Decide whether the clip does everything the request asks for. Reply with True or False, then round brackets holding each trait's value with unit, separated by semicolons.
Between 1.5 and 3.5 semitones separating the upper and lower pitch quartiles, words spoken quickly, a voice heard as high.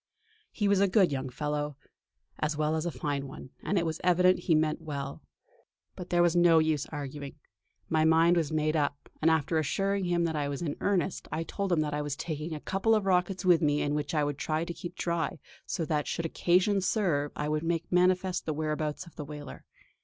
False (3.0 semitones; 220 wpm; 160 Hz)